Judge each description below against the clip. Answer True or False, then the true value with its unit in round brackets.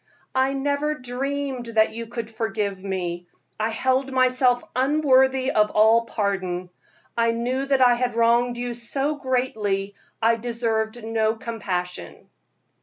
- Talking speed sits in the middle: False (130 wpm)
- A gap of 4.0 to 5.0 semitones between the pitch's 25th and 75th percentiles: False (3.1 semitones)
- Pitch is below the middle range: False (235 Hz)